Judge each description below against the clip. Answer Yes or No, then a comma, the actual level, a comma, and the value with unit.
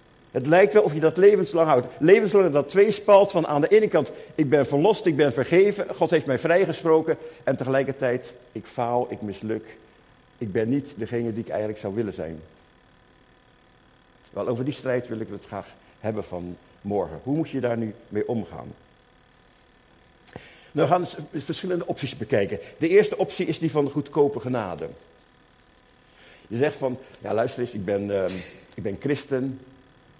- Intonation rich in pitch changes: Yes, wide, 6.1 semitones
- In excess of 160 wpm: Yes, average, 175 wpm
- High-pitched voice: No, low, 130 Hz